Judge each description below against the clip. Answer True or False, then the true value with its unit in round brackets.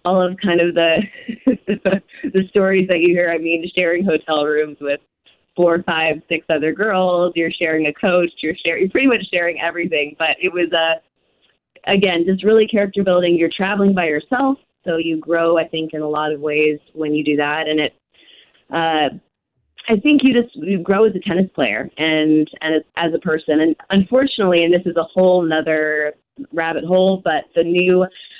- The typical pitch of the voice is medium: True (170 Hz)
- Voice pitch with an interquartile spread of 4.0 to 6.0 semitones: False (3.1 semitones)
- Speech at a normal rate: True (195 wpm)